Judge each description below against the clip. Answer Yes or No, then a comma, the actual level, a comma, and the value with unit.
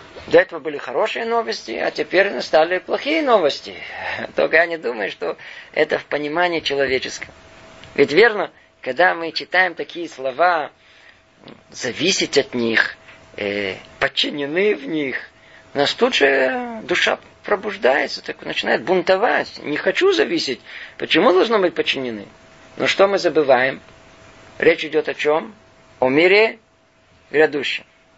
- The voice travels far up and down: Yes, wide, 6.1 semitones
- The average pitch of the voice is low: No, medium, 160 Hz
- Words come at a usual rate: Yes, average, 125 wpm